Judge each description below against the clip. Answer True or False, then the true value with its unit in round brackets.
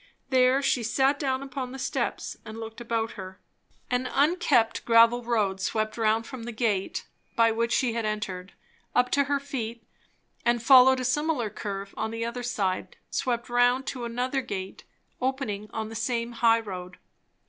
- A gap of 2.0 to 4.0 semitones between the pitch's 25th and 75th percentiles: True (2.7 semitones)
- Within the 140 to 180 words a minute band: True (170 wpm)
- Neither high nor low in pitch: False (235 Hz)